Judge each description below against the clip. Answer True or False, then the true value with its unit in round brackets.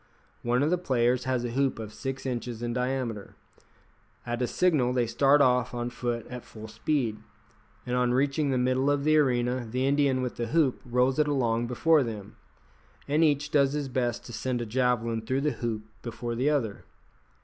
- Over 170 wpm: True (195 wpm)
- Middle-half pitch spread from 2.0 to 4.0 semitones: True (2.6 semitones)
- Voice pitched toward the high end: False (125 Hz)